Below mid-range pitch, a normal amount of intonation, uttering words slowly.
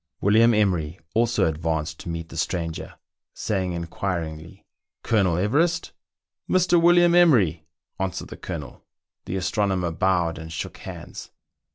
Yes: very low, 90 Hz; average, 4.7 semitones; slow, 130 wpm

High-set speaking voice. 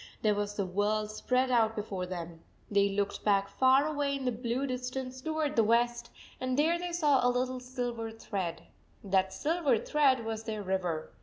Yes: high, 235 Hz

